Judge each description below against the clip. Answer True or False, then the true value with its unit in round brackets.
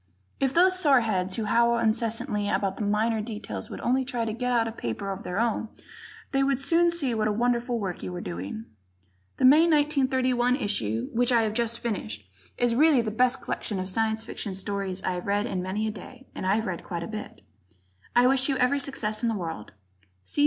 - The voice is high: True (225 Hz)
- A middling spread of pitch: True (4.0 semitones)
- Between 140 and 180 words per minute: False (200 wpm)